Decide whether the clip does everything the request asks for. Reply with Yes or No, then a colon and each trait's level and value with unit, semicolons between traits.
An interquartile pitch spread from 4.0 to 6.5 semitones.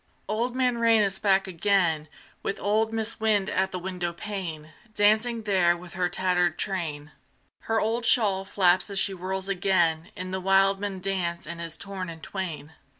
No: average, 2.9 semitones